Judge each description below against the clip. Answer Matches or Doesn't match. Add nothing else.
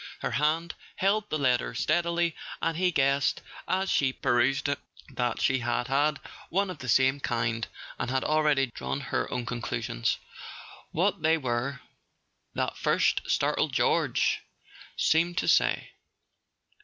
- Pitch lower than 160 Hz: Matches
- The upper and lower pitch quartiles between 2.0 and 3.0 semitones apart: Doesn't match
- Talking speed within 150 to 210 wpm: Doesn't match